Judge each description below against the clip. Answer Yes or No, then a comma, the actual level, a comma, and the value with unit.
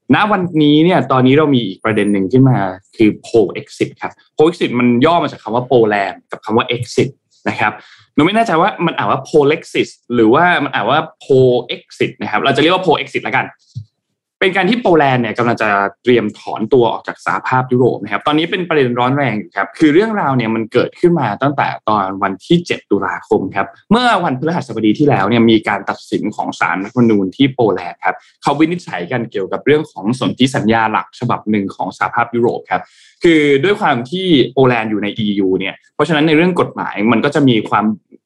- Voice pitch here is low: Yes, low, 125 Hz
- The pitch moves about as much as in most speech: No, wide, 5.9 semitones